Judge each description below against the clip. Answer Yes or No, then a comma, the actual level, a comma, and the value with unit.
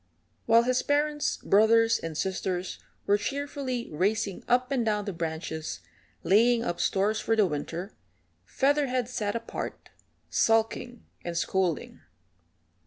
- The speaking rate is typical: No, slow, 120 wpm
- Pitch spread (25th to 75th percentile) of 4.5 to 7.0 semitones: Yes, average, 4.8 semitones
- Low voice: No, high, 220 Hz